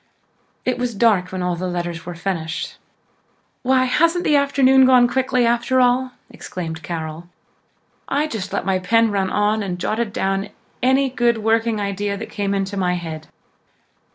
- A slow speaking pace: No, average, 160 wpm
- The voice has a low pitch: No, high, 210 Hz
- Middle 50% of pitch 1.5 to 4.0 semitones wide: No, wide, 5.5 semitones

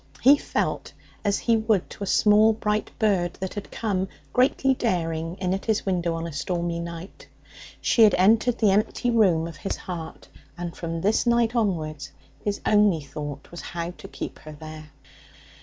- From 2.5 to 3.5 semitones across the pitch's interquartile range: No, average, 4.5 semitones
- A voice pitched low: No, medium, 185 Hz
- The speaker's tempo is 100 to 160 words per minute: No, average, 175 wpm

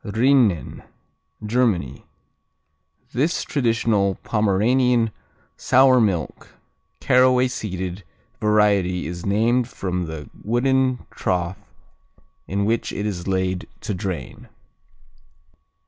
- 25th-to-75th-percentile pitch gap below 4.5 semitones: No, average, 5.0 semitones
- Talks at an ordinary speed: No, slow, 85 wpm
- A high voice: No, low, 105 Hz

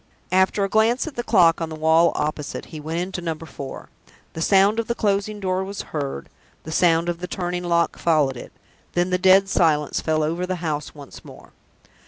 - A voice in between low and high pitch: Yes, medium, 175 Hz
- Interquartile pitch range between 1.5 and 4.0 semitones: Yes, average, 3.3 semitones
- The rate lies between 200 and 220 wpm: Yes, fast, 205 wpm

